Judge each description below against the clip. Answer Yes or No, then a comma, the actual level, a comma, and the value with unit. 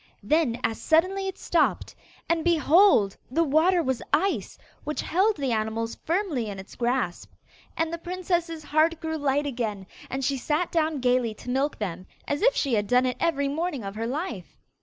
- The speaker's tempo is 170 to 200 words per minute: Yes, average, 180 wpm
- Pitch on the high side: Yes, very high, 290 Hz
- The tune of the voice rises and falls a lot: Yes, wide, 5.8 semitones